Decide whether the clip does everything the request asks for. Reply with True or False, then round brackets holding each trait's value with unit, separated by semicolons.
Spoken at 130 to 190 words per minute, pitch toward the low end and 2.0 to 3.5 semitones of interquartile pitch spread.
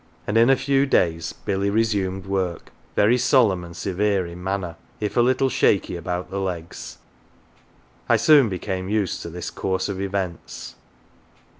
True (155 wpm; 95 Hz; 3.2 semitones)